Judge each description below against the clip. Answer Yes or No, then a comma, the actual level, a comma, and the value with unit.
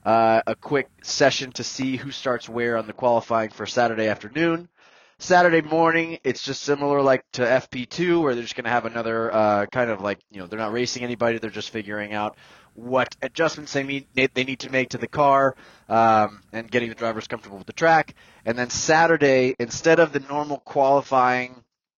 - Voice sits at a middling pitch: No, low, 125 Hz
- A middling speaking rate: Yes, average, 195 wpm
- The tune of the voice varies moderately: Yes, average, 3.6 semitones